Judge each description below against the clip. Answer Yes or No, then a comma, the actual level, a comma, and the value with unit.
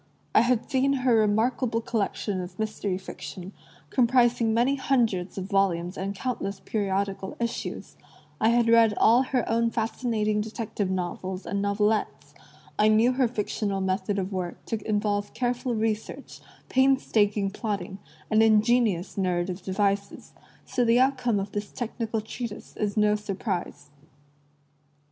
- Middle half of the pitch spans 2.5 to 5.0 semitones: Yes, average, 3.1 semitones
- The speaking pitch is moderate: No, high, 215 Hz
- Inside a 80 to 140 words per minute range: Yes, slow, 135 wpm